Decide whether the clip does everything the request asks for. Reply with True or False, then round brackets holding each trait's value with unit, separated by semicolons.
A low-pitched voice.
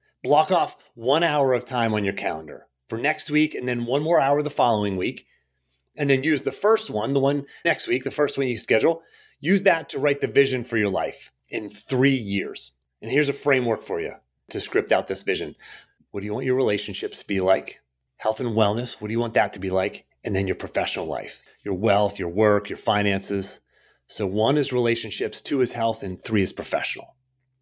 True (115 Hz)